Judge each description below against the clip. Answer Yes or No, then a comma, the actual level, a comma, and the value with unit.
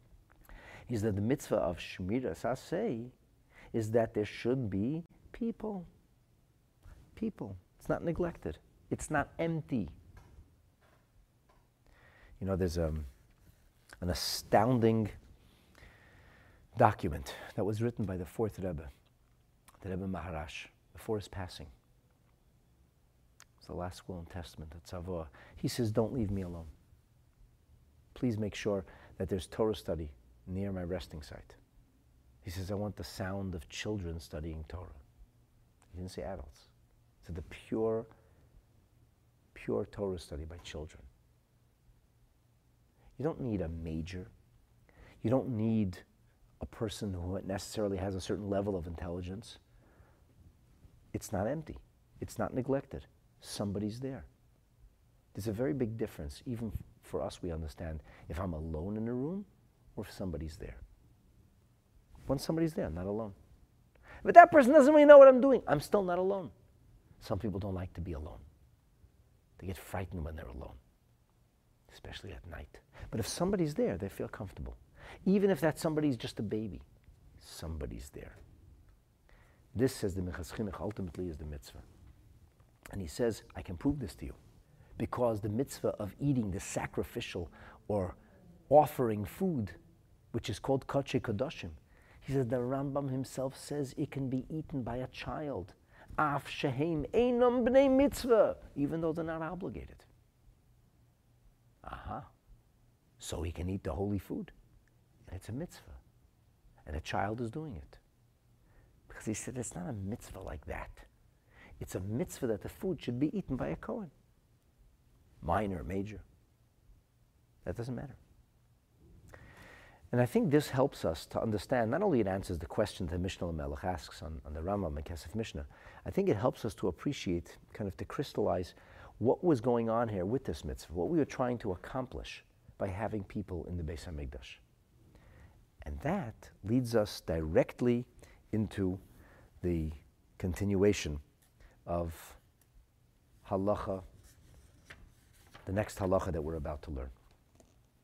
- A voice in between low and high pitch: No, low, 100 Hz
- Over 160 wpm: No, average, 145 wpm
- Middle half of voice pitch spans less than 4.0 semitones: No, wide, 5.4 semitones